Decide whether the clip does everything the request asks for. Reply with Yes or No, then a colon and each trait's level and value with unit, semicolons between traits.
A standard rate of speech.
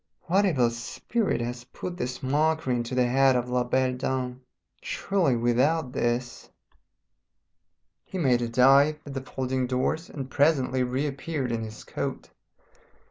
Yes: average, 145 wpm